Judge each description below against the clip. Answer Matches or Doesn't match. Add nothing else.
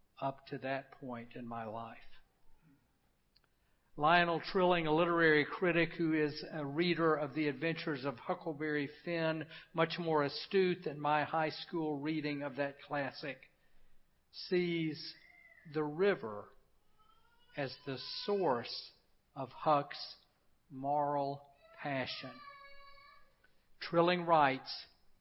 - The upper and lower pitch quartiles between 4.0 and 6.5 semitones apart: Doesn't match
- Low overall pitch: Doesn't match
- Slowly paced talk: Matches